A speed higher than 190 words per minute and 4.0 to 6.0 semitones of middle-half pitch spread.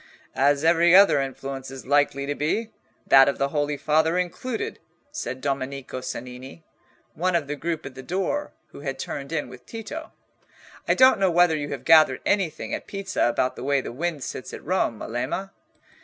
No: average, 185 wpm; average, 4.5 semitones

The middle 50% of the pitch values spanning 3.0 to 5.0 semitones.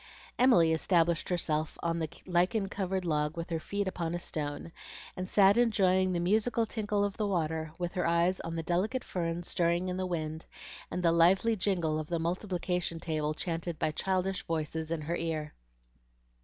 No: narrow, 2.5 semitones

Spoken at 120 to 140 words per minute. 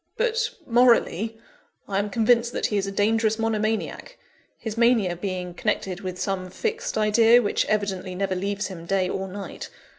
No: average, 160 wpm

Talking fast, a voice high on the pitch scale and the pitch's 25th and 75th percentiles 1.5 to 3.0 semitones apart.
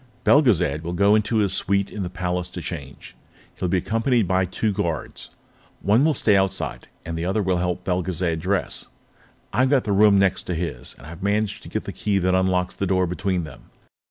No: fast, 210 wpm; very low, 95 Hz; narrow, 2.4 semitones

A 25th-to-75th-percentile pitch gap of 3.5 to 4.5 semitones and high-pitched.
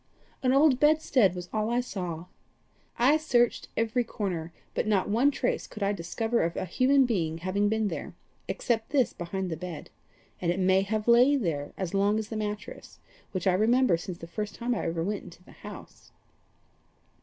No: average, 4.9 semitones; high, 210 Hz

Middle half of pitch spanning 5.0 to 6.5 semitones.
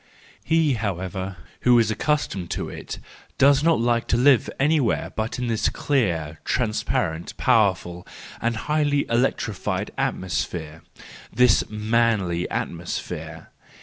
Yes: wide, 5.5 semitones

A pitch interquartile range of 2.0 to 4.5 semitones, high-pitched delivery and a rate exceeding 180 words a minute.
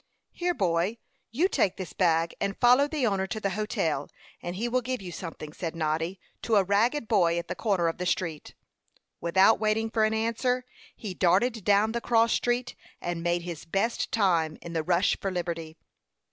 No: average, 5.0 semitones; high, 195 Hz; average, 190 wpm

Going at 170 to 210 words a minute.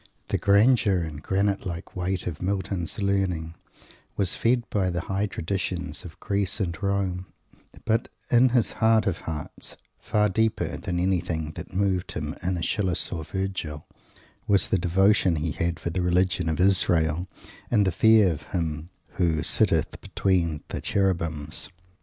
No: average, 155 wpm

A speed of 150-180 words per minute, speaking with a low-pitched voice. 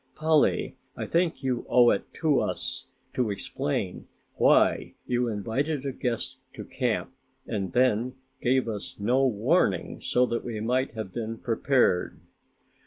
No: average, 140 wpm; low, 120 Hz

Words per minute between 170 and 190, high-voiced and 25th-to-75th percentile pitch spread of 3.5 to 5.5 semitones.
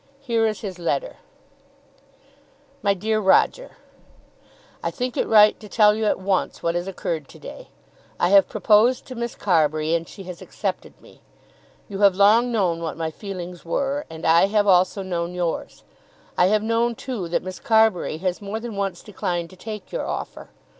Yes: average, 180 wpm; high, 195 Hz; average, 4.0 semitones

